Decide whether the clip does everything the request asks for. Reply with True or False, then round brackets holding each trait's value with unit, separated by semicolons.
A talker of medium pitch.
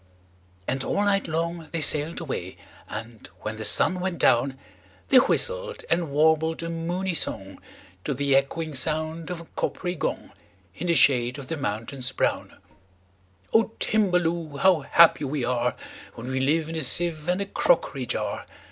True (155 Hz)